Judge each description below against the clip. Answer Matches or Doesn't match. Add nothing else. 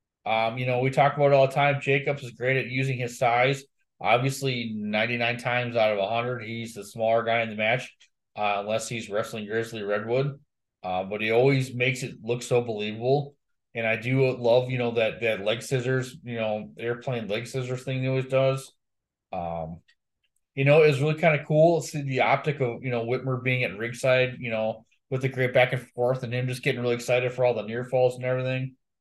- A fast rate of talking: Matches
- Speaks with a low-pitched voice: Matches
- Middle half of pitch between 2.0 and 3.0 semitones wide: Matches